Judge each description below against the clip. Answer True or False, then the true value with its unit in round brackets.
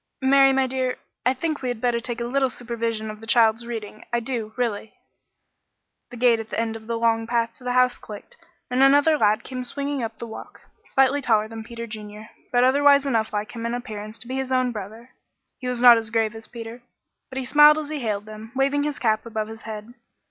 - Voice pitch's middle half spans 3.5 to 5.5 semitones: False (2.8 semitones)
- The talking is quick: True (220 wpm)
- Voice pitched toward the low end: False (235 Hz)